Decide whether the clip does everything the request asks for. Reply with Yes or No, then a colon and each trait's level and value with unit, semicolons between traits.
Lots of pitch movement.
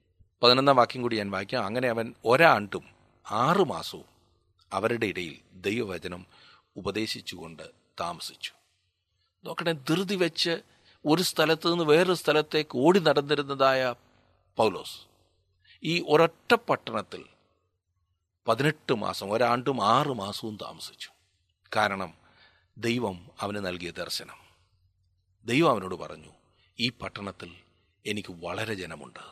Yes: wide, 7.4 semitones